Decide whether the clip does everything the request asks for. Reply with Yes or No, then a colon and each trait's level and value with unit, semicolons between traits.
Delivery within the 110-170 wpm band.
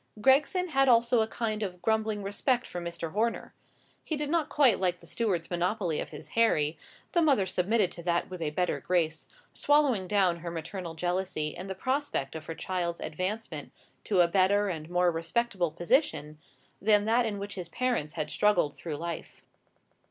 No: average, 180 wpm